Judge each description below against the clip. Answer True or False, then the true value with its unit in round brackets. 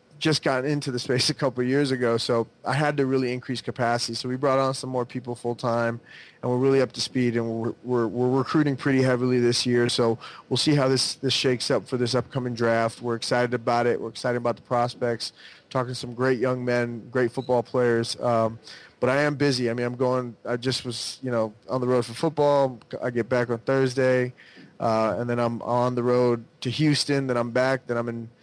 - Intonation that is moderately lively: False (1.8 semitones)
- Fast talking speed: True (235 wpm)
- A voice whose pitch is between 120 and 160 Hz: True (125 Hz)